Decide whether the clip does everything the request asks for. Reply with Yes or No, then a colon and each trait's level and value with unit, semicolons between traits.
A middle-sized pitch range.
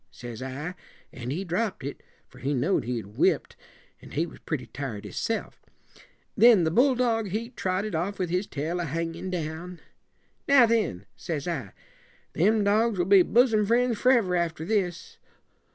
No: wide, 5.9 semitones